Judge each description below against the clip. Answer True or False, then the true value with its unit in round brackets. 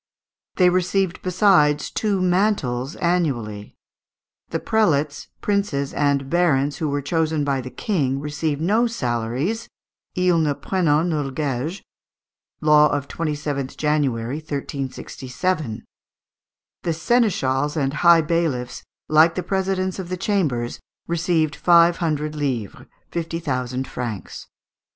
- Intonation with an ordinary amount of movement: True (4.4 semitones)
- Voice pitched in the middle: True (155 Hz)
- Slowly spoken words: True (115 wpm)